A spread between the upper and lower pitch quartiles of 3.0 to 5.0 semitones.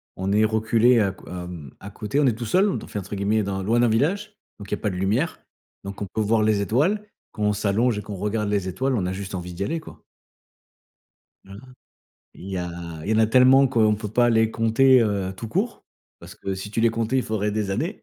Yes: average, 3.3 semitones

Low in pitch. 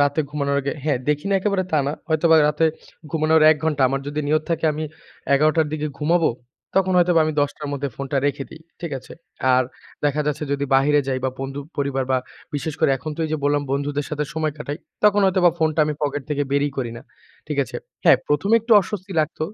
No: medium, 150 Hz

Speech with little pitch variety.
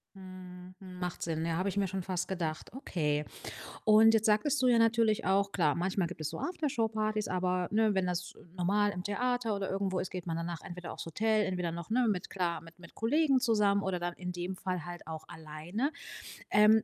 No: average, 3.5 semitones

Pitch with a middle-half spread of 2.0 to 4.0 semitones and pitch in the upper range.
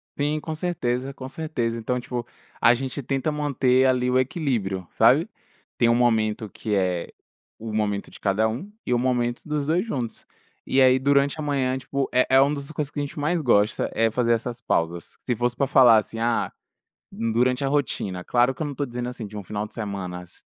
No: average, 3.6 semitones; low, 125 Hz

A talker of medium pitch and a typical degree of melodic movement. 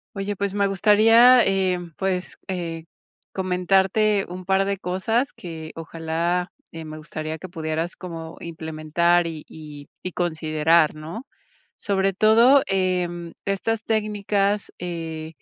Yes: medium, 180 Hz; average, 3.4 semitones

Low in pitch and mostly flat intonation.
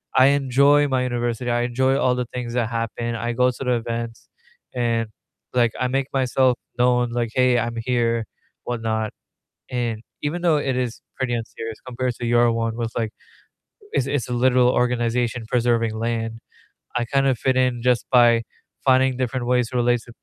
Yes: low, 120 Hz; narrow, 1.6 semitones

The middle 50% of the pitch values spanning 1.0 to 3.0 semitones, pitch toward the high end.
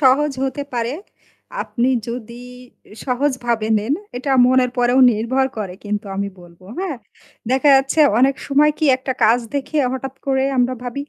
Yes: narrow, 2.5 semitones; very high, 255 Hz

